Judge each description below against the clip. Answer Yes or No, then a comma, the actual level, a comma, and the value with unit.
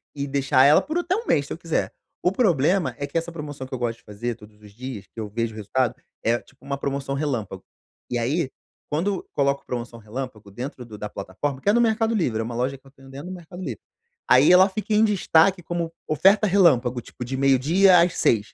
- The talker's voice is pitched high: No, medium, 140 Hz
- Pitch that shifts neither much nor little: No, wide, 6.3 semitones